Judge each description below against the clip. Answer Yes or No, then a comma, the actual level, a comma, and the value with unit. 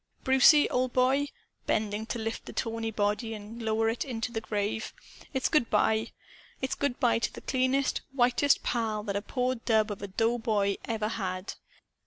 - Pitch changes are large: No, average, 2.9 semitones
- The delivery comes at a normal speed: Yes, average, 175 wpm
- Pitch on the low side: No, high, 225 Hz